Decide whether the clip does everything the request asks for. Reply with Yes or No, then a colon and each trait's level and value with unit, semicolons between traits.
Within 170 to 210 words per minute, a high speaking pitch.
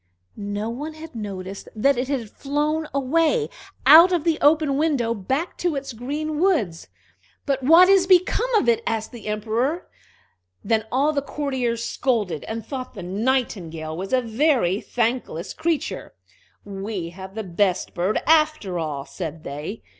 No: average, 155 wpm; high, 245 Hz